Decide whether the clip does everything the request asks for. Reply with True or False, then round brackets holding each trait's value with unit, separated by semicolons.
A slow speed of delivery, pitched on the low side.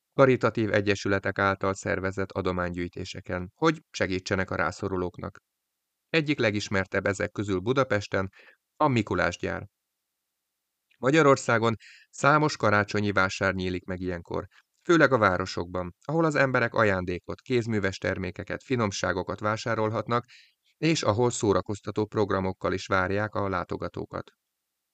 True (100 wpm; 100 Hz)